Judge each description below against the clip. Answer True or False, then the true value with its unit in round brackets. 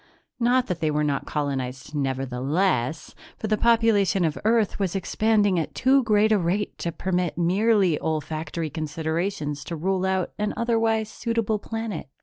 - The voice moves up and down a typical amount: False (5.8 semitones)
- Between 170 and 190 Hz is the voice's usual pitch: True (185 Hz)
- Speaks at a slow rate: False (150 wpm)